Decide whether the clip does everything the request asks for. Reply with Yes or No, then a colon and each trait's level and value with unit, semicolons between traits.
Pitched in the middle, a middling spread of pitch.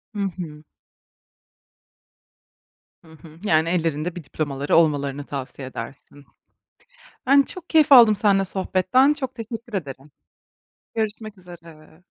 No: medium, 175 Hz; wide, 6.3 semitones